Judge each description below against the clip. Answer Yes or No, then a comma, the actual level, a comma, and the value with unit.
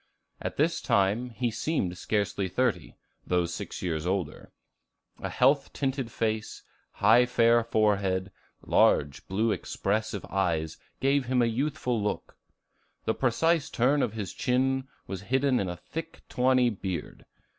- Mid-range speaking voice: No, low, 115 Hz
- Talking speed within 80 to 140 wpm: Yes, slow, 135 wpm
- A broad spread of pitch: No, average, 4.9 semitones